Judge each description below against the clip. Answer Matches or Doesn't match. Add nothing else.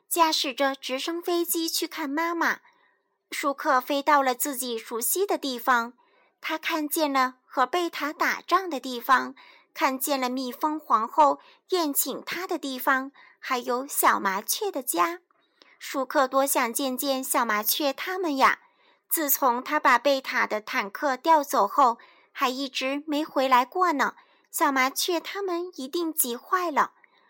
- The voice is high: Matches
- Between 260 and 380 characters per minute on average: Doesn't match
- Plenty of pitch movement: Doesn't match